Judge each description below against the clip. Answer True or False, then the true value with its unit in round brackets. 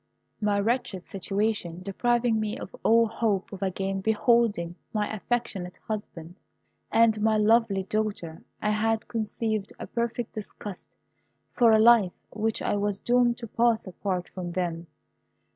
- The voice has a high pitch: True (215 Hz)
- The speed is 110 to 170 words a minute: True (140 wpm)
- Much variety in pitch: False (2.9 semitones)